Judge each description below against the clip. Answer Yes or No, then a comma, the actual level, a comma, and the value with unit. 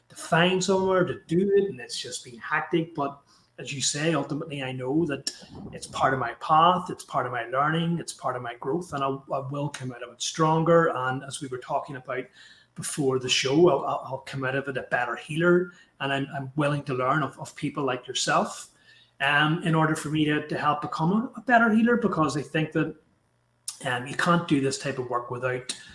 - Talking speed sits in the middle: No, fast, 225 wpm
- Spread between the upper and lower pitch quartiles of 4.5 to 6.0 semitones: No, average, 3.8 semitones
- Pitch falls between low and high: Yes, medium, 150 Hz